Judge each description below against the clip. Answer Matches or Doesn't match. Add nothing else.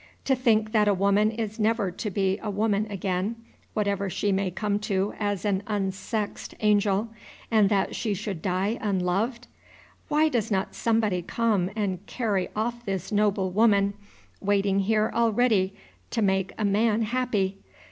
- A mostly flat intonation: Matches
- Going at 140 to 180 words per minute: Matches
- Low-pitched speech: Doesn't match